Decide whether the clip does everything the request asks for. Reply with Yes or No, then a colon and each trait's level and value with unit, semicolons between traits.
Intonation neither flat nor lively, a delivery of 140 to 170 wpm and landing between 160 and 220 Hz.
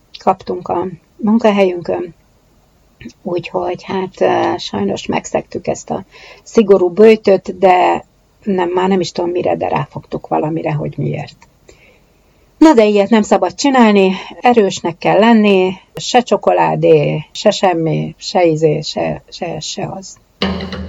No: average, 3.1 semitones; average, 120 wpm; medium, 185 Hz